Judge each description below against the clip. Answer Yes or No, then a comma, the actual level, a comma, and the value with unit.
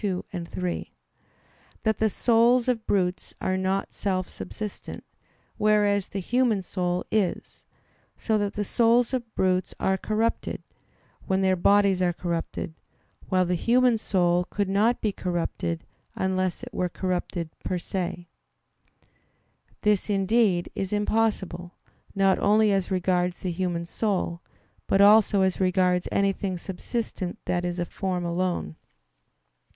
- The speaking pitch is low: No, high, 190 Hz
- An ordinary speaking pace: No, slow, 130 wpm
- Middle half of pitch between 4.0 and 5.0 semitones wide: No, average, 2.8 semitones